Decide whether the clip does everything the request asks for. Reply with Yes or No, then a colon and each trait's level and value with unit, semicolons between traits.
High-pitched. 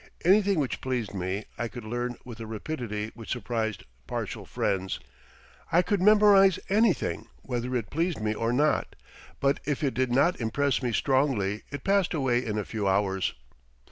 No: low, 125 Hz